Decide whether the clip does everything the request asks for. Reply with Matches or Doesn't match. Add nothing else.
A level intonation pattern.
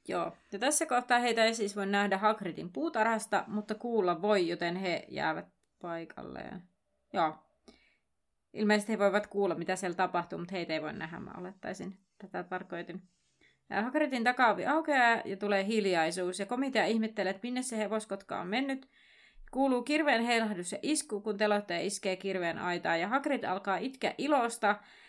Doesn't match